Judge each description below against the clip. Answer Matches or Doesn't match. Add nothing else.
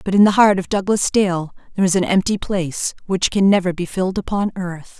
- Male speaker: Doesn't match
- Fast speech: Matches